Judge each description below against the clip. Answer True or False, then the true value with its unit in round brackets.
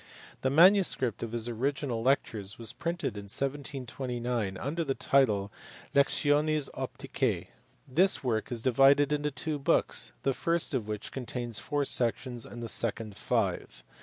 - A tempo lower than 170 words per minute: True (140 wpm)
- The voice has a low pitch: True (130 Hz)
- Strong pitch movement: False (4.0 semitones)